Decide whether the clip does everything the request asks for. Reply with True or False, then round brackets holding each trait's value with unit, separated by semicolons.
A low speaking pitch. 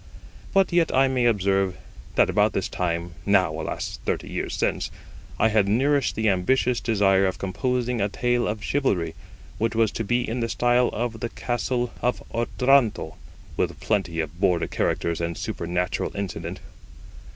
True (110 Hz)